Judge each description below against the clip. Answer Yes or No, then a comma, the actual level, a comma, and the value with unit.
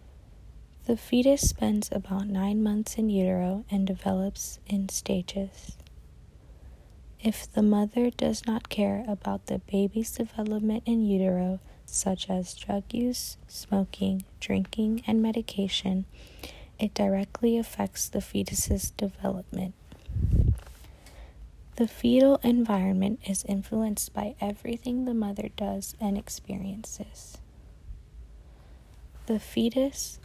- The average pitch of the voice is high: Yes, high, 200 Hz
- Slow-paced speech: Yes, slow, 105 wpm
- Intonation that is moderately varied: Yes, average, 3.0 semitones